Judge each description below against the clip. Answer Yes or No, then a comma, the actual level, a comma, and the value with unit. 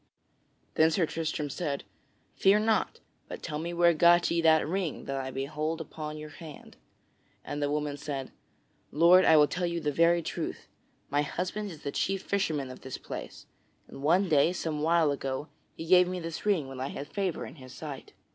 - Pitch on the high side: No, medium, 160 Hz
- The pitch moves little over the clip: No, average, 3.0 semitones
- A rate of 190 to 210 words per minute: Yes, average, 195 wpm